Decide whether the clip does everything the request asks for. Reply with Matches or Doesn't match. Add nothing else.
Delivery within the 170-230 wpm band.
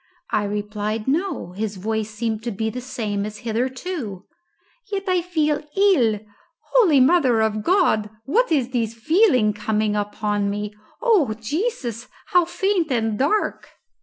Doesn't match